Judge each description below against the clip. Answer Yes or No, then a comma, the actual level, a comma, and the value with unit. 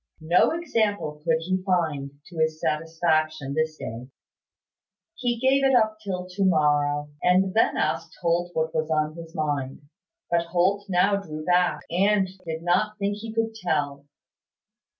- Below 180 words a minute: Yes, average, 150 wpm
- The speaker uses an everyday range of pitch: Yes, average, 4.3 semitones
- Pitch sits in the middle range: Yes, medium, 170 Hz